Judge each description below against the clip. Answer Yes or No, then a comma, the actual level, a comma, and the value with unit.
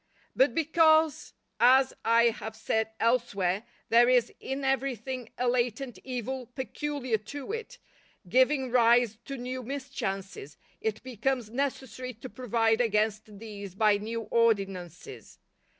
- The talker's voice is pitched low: No, high, 240 Hz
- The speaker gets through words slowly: Yes, slow, 120 wpm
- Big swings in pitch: No, average, 3.3 semitones